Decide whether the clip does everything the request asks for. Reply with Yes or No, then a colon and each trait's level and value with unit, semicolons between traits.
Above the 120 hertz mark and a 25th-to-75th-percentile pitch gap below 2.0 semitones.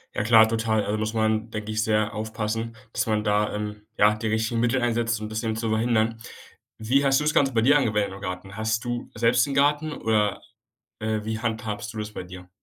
No: low, 110 Hz; narrow, 1.4 semitones